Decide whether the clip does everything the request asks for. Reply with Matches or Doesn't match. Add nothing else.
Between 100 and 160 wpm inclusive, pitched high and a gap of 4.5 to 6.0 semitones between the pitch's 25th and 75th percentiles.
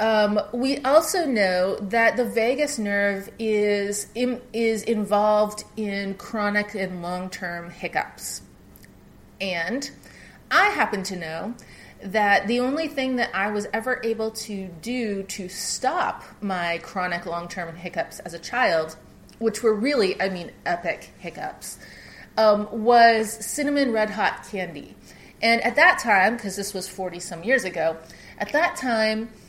Doesn't match